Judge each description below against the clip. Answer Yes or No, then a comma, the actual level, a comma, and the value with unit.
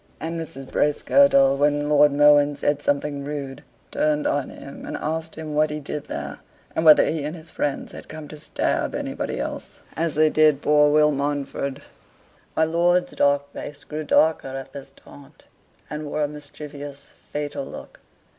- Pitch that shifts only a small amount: Yes, narrow, 1.3 semitones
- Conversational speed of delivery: Yes, average, 175 wpm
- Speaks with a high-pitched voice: No, medium, 150 Hz